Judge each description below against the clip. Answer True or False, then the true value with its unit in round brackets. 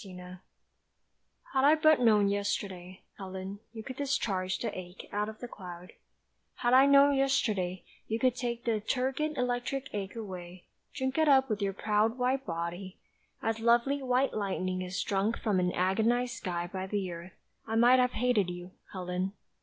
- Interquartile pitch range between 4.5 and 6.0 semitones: True (5.2 semitones)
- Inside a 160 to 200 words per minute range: True (170 wpm)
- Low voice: False (215 Hz)